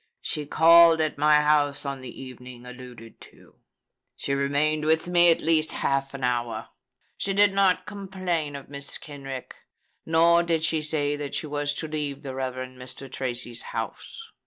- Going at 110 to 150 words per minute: No, average, 165 wpm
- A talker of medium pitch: Yes, medium, 145 Hz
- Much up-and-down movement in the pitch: No, average, 3.4 semitones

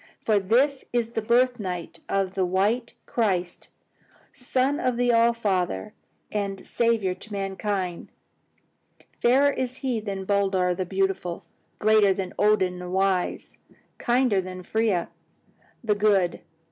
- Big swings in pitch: No, average, 3.9 semitones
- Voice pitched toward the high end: Yes, high, 200 Hz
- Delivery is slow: Yes, slow, 130 wpm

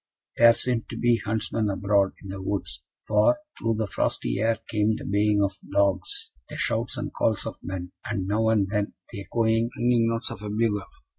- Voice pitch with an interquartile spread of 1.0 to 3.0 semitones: Yes, narrow, 2.5 semitones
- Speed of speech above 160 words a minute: Yes, average, 195 wpm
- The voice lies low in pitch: Yes, low, 105 Hz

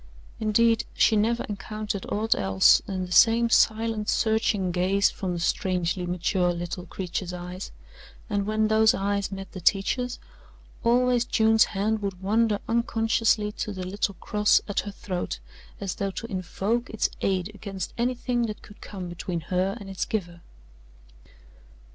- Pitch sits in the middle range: No, high, 205 Hz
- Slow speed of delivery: No, average, 150 wpm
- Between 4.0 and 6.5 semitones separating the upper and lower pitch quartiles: No, average, 3.2 semitones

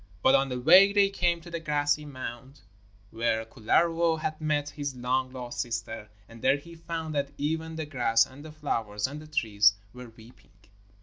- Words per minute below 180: No, average, 185 wpm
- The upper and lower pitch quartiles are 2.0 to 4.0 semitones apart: No, average, 4.7 semitones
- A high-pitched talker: No, medium, 145 Hz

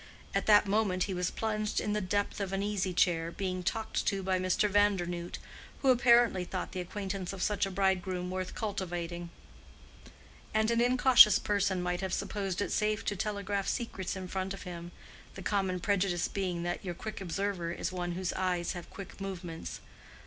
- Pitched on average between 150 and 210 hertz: Yes, high, 190 Hz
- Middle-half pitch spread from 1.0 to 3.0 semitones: Yes, narrow, 2.4 semitones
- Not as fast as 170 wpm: No, average, 180 wpm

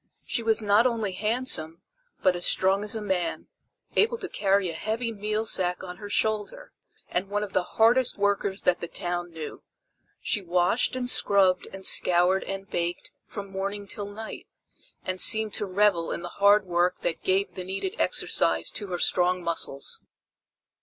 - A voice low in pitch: No, high, 195 Hz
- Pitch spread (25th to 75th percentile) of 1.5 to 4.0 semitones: Yes, average, 3.0 semitones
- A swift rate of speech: No, average, 175 wpm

